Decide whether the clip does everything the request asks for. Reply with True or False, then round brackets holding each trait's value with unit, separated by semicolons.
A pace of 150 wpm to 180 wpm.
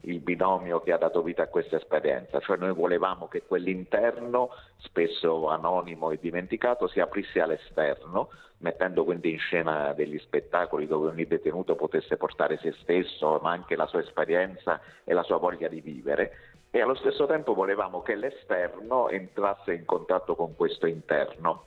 True (160 wpm)